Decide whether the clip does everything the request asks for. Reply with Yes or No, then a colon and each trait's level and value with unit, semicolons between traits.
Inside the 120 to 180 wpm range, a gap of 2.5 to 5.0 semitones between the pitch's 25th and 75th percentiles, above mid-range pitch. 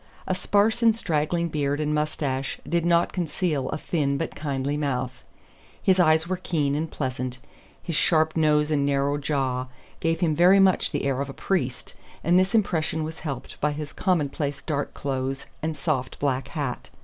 No: average, 175 wpm; average, 3.3 semitones; medium, 150 Hz